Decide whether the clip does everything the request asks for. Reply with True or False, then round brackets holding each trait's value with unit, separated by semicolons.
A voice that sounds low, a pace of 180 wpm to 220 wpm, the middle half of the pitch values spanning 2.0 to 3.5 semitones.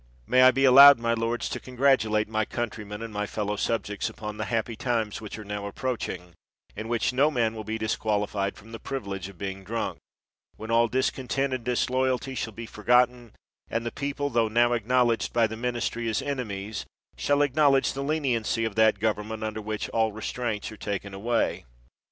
True (115 Hz; 185 wpm; 2.8 semitones)